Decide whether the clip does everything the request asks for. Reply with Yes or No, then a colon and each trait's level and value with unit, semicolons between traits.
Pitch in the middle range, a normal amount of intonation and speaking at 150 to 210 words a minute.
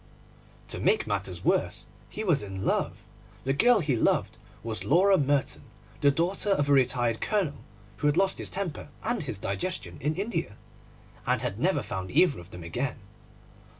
No: medium, 145 Hz; wide, 8.4 semitones; average, 170 wpm